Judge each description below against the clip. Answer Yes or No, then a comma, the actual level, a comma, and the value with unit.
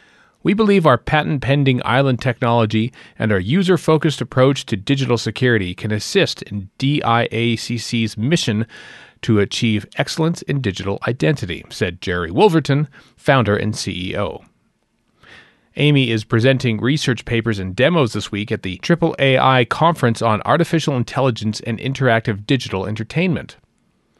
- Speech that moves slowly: Yes, slow, 130 wpm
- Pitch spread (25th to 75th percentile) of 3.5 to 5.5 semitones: Yes, average, 4.4 semitones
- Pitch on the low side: Yes, low, 120 Hz